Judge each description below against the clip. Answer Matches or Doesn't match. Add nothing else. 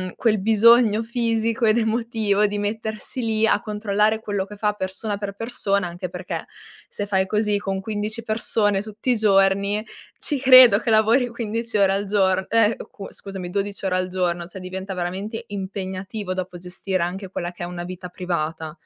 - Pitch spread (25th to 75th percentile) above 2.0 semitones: Matches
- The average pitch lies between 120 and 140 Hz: Doesn't match